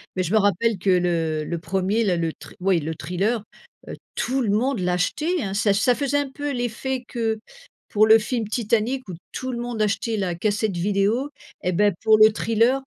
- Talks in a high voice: Yes, high, 215 Hz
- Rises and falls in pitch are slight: No, average, 4.5 semitones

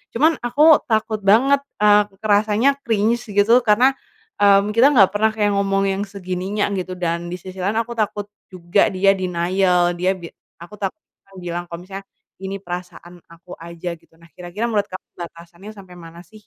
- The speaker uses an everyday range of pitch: Yes, average, 3.2 semitones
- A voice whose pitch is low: No, high, 195 Hz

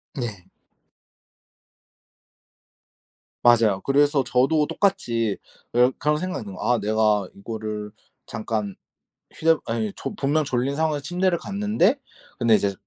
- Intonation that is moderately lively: No, wide, 6.1 semitones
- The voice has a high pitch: No, low, 125 Hz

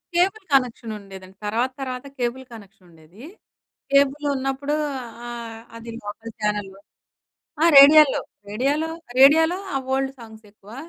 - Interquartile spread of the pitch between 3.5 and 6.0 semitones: Yes, average, 4.8 semitones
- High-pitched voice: Yes, high, 240 Hz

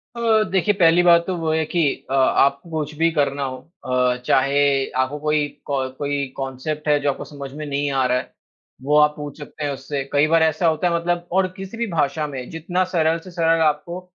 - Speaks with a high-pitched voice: No, medium, 150 Hz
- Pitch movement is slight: No, average, 3.2 semitones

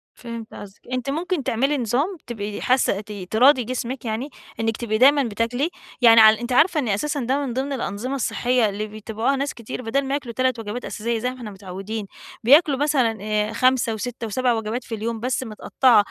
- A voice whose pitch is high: Yes, high, 240 Hz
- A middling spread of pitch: Yes, average, 3.3 semitones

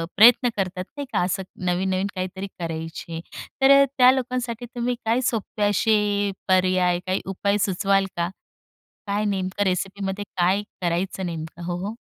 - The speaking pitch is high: Yes, high, 195 Hz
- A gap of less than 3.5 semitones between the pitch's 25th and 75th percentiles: Yes, average, 2.9 semitones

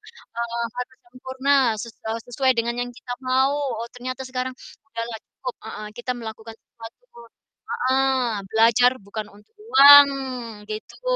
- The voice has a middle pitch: No, high, 245 Hz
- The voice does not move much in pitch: Yes, narrow, 2.2 semitones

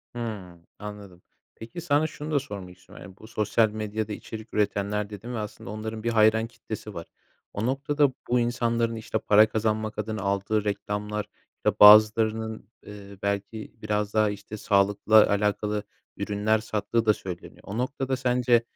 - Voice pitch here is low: Yes, low, 110 Hz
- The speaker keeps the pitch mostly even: Yes, narrow, 1.8 semitones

